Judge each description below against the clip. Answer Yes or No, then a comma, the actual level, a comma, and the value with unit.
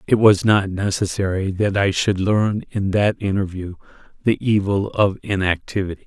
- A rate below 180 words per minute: Yes, average, 150 wpm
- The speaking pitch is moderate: No, low, 100 Hz